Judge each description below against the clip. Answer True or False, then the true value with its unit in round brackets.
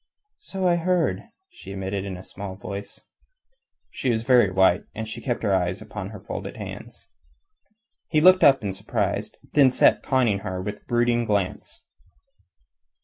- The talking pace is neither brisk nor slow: True (160 wpm)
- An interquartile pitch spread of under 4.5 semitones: False (5.3 semitones)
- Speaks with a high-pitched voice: False (105 Hz)